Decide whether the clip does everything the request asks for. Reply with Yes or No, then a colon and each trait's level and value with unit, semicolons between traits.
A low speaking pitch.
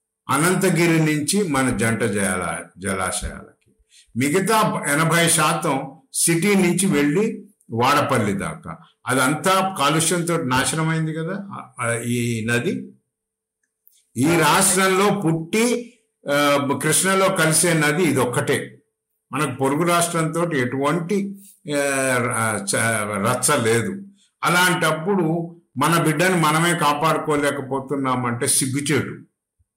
No: medium, 155 Hz